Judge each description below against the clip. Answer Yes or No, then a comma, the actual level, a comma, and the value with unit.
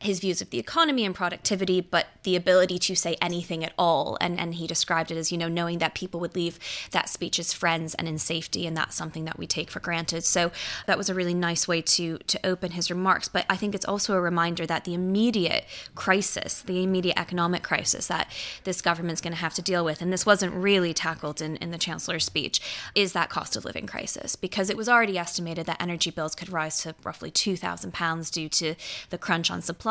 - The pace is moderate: No, fast, 230 wpm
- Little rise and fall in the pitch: Yes, narrow, 2.0 semitones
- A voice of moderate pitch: Yes, medium, 175 Hz